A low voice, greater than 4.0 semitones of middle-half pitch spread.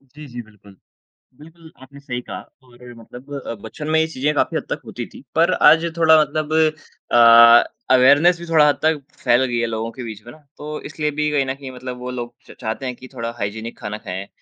Yes: low, 130 Hz; average, 4.4 semitones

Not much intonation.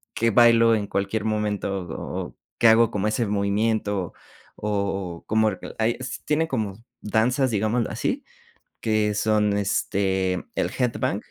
Yes: narrow, 2.3 semitones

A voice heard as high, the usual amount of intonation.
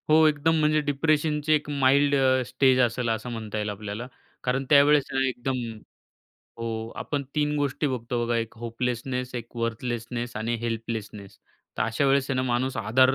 No: low, 125 Hz; average, 3.5 semitones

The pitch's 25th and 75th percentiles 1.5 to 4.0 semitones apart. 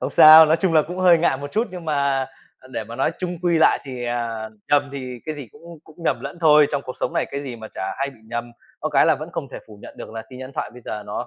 No: average, 4.8 semitones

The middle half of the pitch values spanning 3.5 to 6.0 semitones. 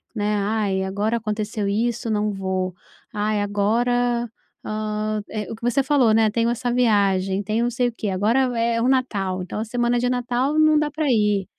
No: average, 2.9 semitones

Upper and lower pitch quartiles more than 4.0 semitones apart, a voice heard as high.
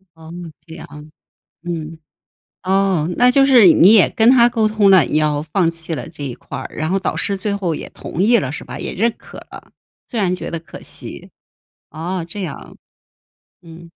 No: average, 4.4 semitones; medium, 180 Hz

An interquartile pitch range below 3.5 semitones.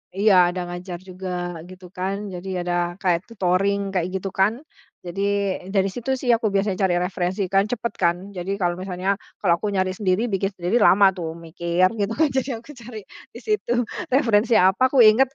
Yes: average, 2.9 semitones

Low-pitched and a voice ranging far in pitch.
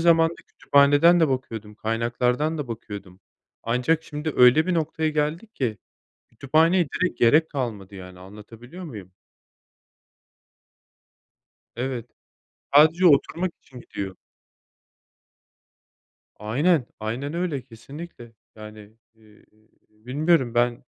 Yes: low, 130 Hz; wide, 6.1 semitones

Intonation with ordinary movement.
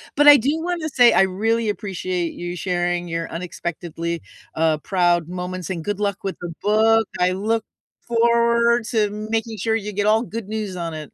Yes: average, 4.2 semitones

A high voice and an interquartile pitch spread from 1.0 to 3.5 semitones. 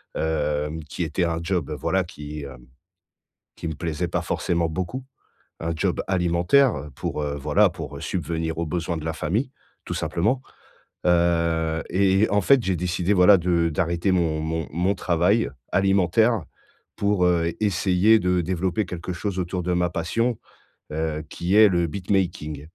No: very low, 85 Hz; average, 2.7 semitones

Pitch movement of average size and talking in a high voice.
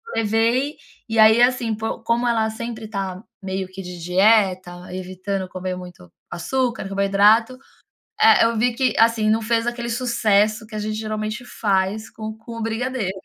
Yes: average, 3.1 semitones; high, 220 Hz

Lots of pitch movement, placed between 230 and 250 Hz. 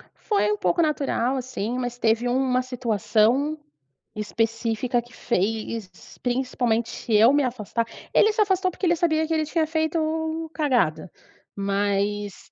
Yes: wide, 5.7 semitones; high, 245 Hz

